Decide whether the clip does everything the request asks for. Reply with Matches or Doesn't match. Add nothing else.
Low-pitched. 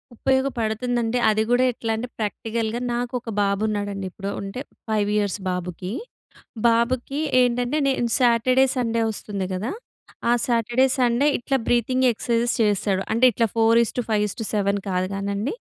Doesn't match